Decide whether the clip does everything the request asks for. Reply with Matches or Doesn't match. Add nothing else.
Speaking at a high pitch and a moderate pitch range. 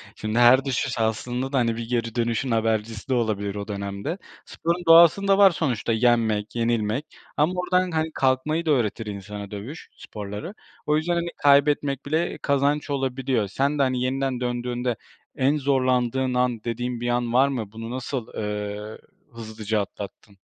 Doesn't match